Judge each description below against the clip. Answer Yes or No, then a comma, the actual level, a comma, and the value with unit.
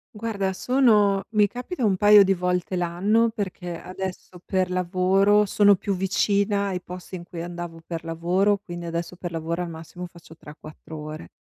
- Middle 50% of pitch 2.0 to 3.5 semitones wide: Yes, average, 2.7 semitones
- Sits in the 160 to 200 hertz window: Yes, medium, 185 Hz